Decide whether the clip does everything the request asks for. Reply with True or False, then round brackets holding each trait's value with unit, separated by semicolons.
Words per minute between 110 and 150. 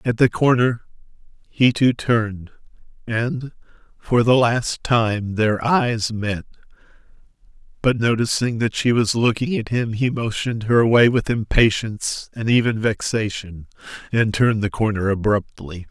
True (135 wpm)